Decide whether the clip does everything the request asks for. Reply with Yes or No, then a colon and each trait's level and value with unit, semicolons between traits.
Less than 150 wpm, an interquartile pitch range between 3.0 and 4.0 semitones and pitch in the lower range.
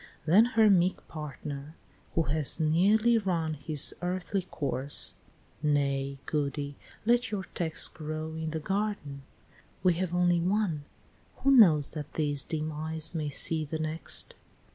No: average, 140 wpm; average, 3.7 semitones; medium, 160 Hz